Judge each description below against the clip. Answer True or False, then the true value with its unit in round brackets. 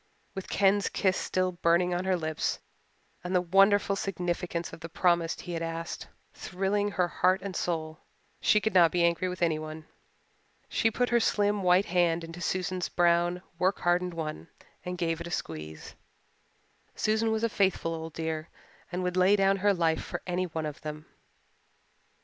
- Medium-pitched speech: True (180 Hz)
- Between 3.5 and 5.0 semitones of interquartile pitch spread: False (2.5 semitones)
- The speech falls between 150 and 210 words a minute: True (170 wpm)